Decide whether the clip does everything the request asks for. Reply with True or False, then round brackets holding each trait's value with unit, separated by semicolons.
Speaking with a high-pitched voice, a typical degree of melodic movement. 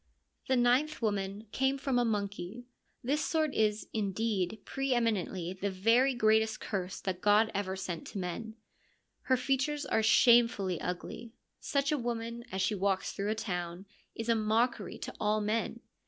True (220 Hz; 3.8 semitones)